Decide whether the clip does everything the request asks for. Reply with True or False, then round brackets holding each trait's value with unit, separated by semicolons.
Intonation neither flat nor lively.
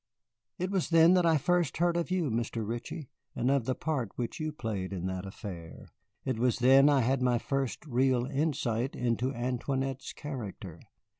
True (4.5 semitones)